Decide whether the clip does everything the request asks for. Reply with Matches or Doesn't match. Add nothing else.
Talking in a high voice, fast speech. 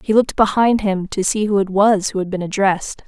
Matches